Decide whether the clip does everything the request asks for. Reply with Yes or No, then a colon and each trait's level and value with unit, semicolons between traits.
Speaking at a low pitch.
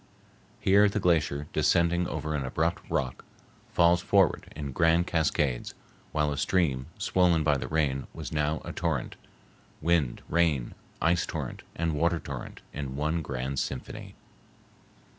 Yes: very low, 80 Hz